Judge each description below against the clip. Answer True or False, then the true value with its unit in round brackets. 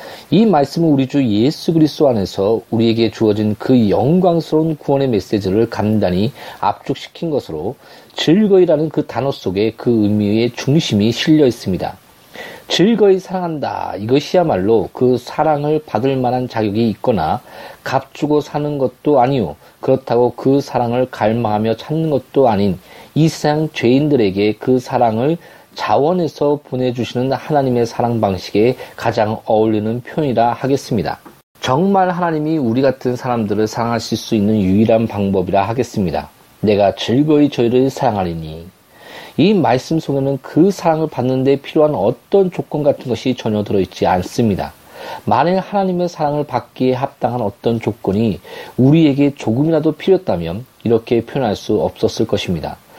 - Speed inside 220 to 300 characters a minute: False (335 characters per minute)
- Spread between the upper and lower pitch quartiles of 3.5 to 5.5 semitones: True (5.1 semitones)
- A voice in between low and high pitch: False (130 Hz)